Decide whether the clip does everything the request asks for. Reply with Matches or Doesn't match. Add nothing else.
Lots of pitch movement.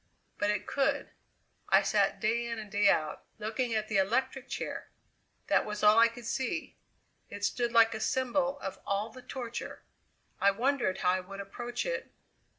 Doesn't match